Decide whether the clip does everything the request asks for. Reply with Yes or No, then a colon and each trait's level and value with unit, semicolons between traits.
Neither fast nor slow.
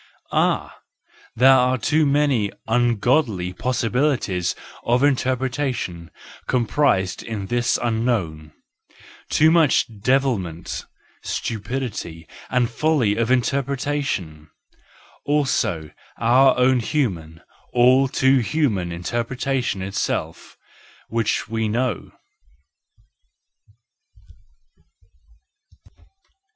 No: slow, 75 wpm